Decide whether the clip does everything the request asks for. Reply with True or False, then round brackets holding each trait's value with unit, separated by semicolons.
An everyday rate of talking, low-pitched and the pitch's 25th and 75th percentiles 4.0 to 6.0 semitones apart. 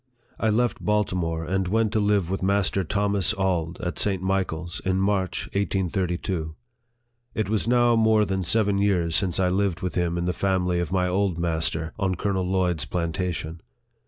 False (170 wpm; 95 Hz; 2.5 semitones)